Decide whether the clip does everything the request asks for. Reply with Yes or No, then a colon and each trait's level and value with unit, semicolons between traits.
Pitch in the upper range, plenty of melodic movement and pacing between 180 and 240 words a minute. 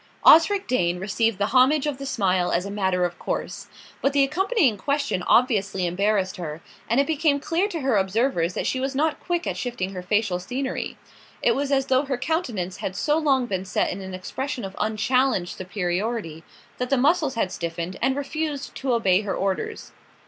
Yes: high, 230 Hz; wide, 6.8 semitones; average, 190 wpm